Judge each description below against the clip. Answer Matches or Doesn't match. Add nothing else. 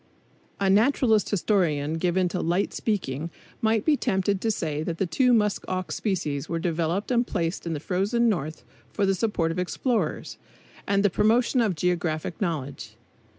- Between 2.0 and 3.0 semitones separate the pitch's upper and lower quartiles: Doesn't match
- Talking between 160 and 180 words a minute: Matches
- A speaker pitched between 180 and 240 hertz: Matches